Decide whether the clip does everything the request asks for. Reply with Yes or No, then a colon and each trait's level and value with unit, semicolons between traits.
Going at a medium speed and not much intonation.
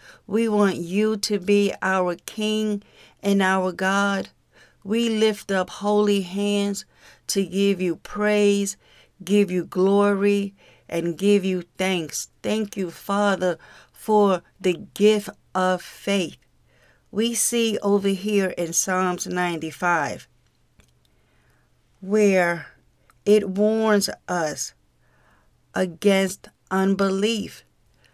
No: slow, 100 wpm; narrow, 2.1 semitones